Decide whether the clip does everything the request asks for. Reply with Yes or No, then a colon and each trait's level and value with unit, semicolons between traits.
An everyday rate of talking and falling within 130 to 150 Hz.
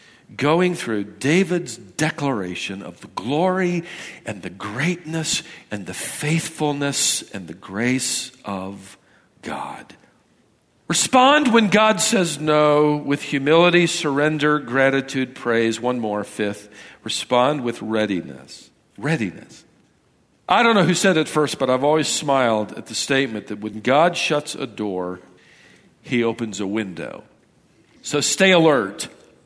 No: slow, 125 wpm; medium, 140 Hz